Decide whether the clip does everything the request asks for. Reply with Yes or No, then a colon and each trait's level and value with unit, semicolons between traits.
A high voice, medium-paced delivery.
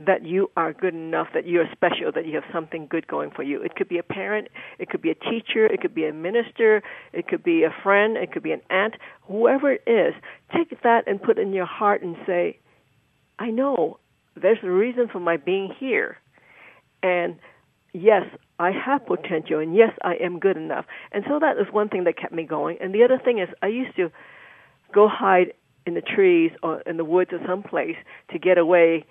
No: high, 195 Hz; fast, 220 wpm